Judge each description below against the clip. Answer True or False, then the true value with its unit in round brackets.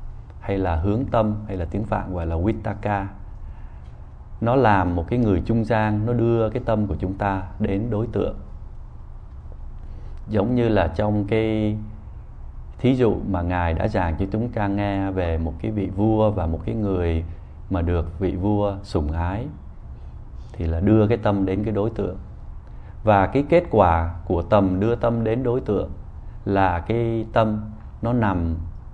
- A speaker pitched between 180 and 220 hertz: False (100 Hz)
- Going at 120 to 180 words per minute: True (170 wpm)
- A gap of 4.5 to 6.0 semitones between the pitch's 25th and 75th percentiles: False (3.9 semitones)